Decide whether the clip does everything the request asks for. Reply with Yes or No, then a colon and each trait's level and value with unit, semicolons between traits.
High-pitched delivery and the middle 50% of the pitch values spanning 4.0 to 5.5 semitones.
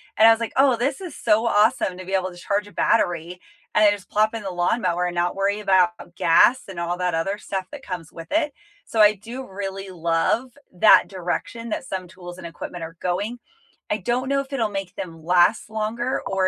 Yes: high, 195 Hz; average, 4.3 semitones